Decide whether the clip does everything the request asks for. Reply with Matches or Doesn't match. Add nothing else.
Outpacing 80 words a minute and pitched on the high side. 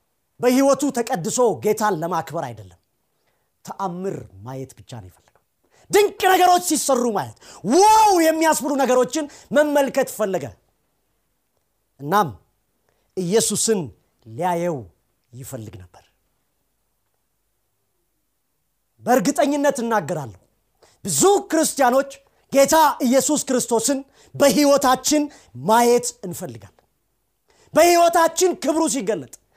Doesn't match